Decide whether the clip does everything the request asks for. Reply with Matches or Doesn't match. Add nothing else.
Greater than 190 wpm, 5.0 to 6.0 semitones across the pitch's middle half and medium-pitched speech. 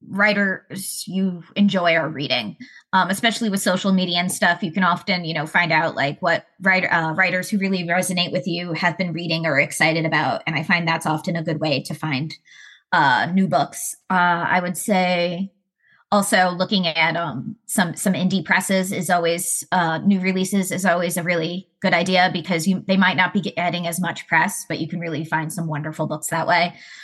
Doesn't match